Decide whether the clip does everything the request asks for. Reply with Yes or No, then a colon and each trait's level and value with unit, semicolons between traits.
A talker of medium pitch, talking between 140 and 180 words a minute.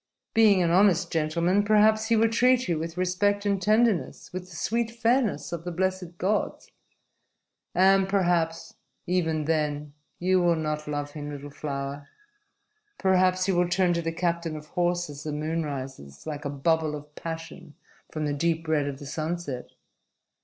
Yes: medium, 170 Hz; average, 165 wpm